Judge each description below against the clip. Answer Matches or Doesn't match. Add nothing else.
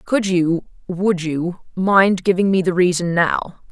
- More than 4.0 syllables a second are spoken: Doesn't match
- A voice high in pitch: Doesn't match